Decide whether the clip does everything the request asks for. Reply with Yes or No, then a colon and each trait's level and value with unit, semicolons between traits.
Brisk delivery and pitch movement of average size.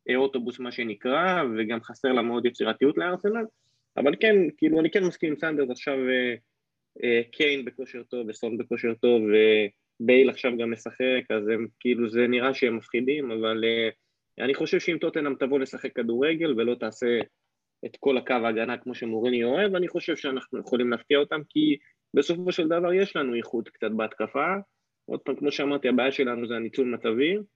Yes: fast, 170 wpm; average, 3.6 semitones